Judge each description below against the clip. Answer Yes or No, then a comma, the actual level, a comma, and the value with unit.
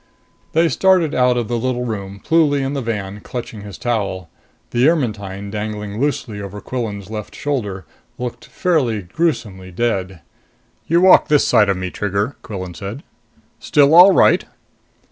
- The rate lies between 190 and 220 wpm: No, average, 150 wpm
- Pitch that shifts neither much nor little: No, wide, 5.7 semitones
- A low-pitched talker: Yes, low, 110 Hz